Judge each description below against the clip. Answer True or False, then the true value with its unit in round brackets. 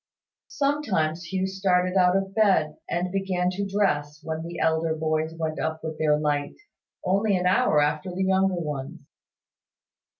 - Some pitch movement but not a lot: True (3.5 semitones)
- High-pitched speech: False (175 Hz)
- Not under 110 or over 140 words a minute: False (155 wpm)